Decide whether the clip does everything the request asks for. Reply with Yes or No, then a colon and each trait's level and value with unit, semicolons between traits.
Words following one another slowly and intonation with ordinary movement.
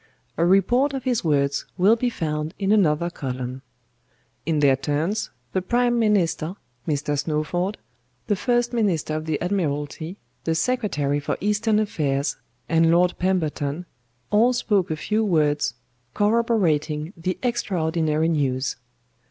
No: slow, 130 wpm; wide, 5.7 semitones